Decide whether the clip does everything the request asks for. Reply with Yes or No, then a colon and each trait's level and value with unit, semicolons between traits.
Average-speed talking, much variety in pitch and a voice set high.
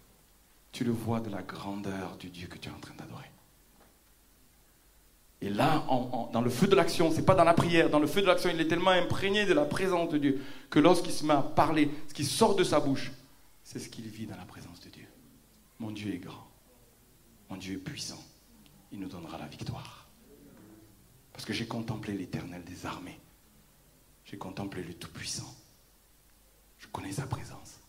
No: average, 200 wpm; wide, 6.6 semitones; low, 125 Hz